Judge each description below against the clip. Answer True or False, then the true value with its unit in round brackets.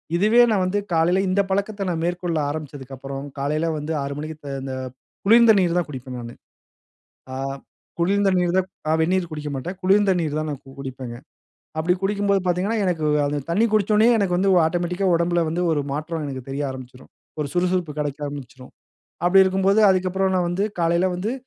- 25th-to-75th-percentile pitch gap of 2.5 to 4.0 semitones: False (4.4 semitones)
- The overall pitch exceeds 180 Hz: False (175 Hz)